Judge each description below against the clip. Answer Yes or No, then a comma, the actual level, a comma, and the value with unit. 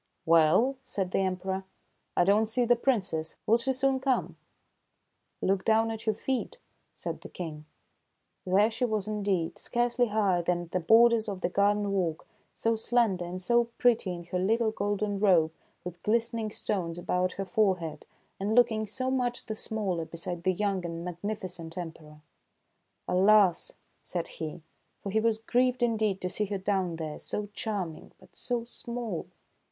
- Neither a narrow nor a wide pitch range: Yes, average, 4.1 semitones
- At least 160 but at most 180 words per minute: Yes, average, 170 wpm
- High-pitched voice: Yes, high, 200 Hz